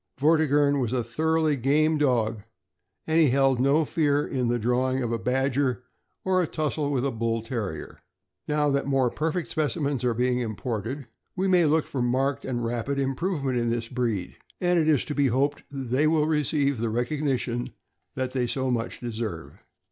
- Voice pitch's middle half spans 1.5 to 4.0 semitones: Yes, average, 3.6 semitones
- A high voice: No, low, 135 Hz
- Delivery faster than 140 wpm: Yes, average, 180 wpm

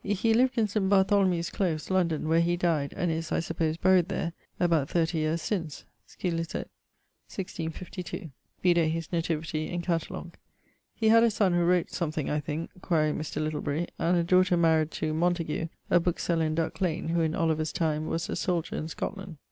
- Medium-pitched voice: Yes, medium, 170 Hz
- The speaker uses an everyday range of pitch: No, narrow, 2.3 semitones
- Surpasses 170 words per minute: Yes, average, 180 wpm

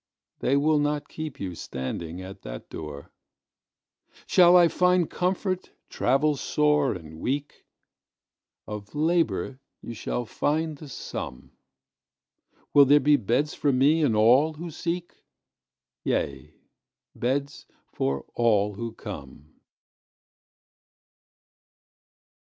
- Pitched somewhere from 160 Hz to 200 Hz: No, low, 135 Hz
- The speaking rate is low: Yes, slow, 95 wpm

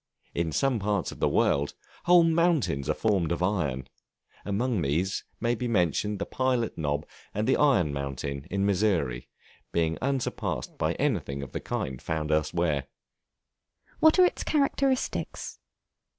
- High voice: No, very low, 95 Hz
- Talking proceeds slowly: No, average, 145 wpm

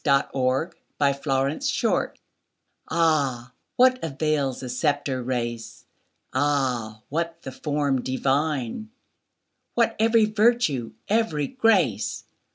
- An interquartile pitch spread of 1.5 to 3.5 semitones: No, average, 4.4 semitones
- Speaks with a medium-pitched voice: Yes, medium, 145 Hz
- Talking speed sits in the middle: No, slow, 85 wpm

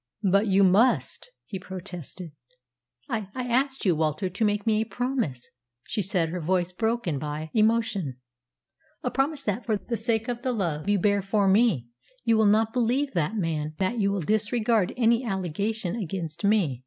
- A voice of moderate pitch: No, high, 205 Hz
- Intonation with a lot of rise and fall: No, average, 4.4 semitones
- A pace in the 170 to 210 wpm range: Yes, average, 175 wpm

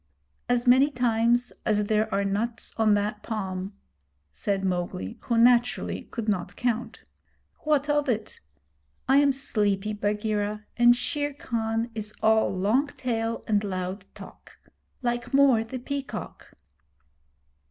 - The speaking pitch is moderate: No, high, 225 Hz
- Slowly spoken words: Yes, slow, 130 wpm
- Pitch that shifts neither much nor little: Yes, average, 3.0 semitones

